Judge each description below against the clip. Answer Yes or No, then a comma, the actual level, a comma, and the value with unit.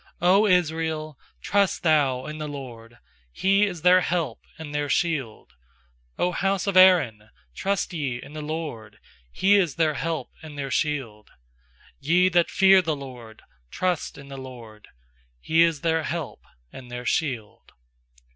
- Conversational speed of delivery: Yes, average, 150 wpm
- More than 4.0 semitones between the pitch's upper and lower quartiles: Yes, average, 5.3 semitones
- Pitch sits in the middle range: Yes, medium, 155 Hz